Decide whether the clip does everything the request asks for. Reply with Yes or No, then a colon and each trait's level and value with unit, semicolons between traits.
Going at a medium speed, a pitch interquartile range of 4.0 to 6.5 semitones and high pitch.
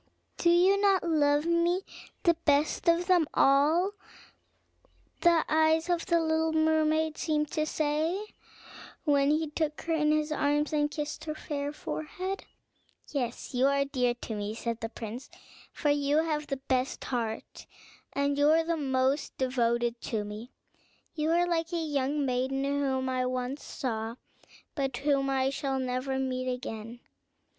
No: average, 155 wpm; average, 3.5 semitones; very high, 290 Hz